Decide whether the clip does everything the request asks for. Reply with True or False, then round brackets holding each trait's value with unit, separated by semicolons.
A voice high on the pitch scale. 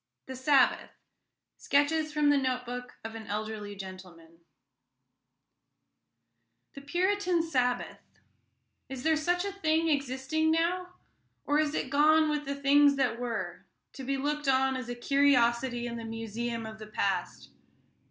True (265 Hz)